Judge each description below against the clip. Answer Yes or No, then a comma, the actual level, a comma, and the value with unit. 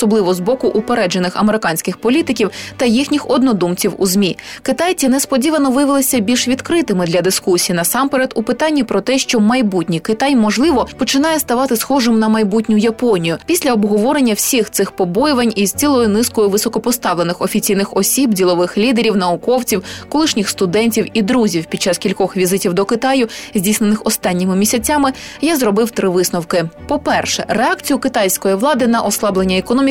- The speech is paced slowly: No, average, 140 wpm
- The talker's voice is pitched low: No, high, 225 Hz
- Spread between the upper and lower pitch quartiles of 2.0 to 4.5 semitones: No, average, 5.1 semitones